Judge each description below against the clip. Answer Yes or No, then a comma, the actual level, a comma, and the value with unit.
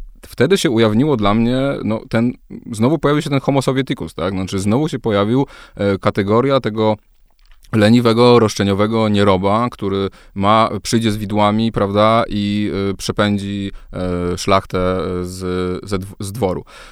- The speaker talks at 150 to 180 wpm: No, average, 135 wpm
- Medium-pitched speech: No, low, 105 Hz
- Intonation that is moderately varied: Yes, average, 3.0 semitones